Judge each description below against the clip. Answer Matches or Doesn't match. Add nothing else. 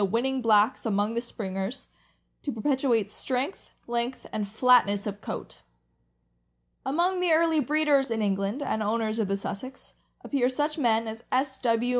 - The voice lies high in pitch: Matches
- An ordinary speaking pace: Matches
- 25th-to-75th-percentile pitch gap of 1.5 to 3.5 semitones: Doesn't match